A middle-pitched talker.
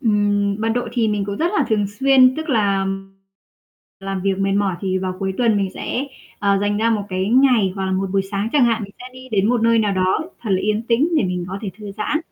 No: high, 205 Hz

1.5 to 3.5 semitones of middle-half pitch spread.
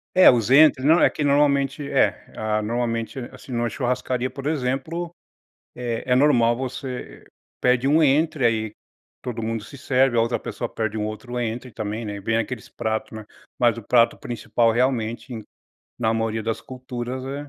Yes: average, 2.9 semitones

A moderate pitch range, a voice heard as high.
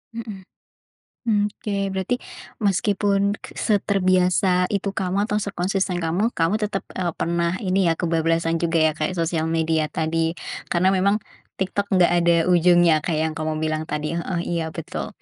No: average, 3.2 semitones; medium, 175 Hz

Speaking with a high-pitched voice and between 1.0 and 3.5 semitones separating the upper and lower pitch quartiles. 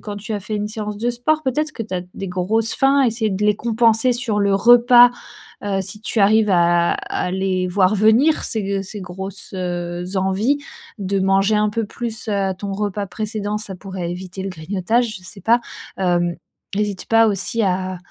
Yes: high, 205 Hz; average, 3.0 semitones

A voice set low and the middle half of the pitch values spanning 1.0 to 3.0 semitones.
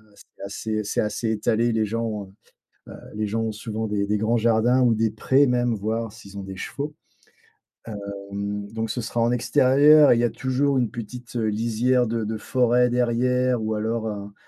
Yes: low, 115 Hz; narrow, 2.5 semitones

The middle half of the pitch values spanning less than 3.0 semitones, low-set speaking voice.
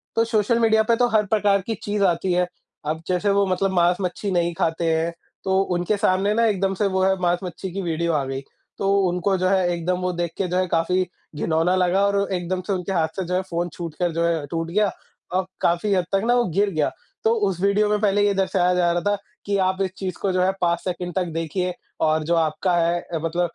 No: narrow, 2.5 semitones; medium, 185 Hz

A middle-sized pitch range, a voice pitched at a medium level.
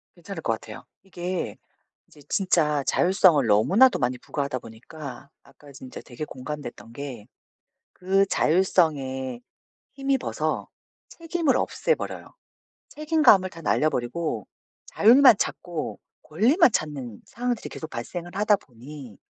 No: wide, 7.2 semitones; medium, 155 Hz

